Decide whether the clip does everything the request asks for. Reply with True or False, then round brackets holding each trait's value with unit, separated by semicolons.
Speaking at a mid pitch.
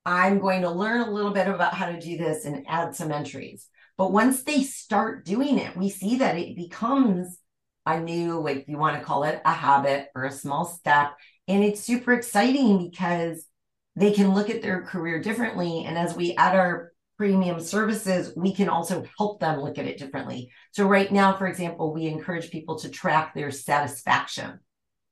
True (175 Hz)